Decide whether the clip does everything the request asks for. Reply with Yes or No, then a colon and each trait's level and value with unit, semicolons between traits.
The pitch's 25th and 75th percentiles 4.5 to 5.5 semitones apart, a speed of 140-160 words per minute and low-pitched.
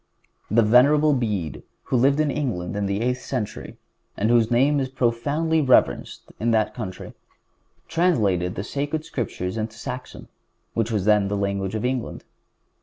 Yes: average, 4.9 semitones; average, 155 wpm; low, 115 Hz